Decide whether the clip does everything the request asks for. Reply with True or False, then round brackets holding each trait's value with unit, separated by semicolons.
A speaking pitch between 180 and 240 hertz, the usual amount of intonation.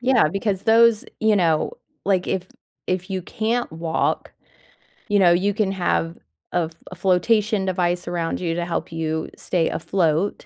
True (185 Hz; 3.1 semitones)